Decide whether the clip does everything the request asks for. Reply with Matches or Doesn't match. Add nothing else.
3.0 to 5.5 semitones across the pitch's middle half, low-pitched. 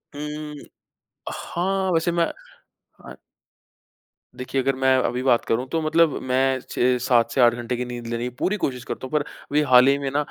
Matches